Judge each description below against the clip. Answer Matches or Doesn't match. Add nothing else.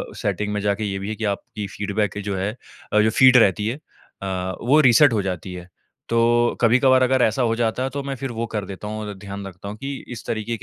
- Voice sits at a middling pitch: Doesn't match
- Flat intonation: Doesn't match